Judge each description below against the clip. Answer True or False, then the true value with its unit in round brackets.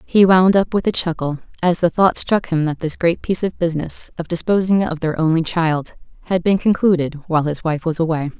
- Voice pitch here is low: False (170 Hz)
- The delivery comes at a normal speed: False (220 wpm)